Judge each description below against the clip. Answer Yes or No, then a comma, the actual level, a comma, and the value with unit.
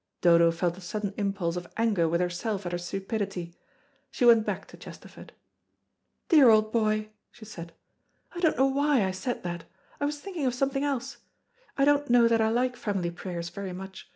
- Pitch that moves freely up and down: Yes, wide, 5.8 semitones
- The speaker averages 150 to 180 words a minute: No, average, 190 wpm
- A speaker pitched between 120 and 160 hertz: No, high, 215 Hz